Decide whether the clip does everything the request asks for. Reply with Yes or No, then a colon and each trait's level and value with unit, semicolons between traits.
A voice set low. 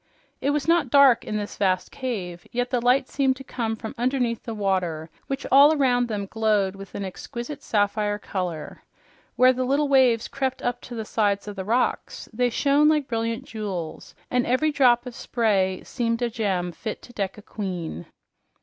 No: high, 230 Hz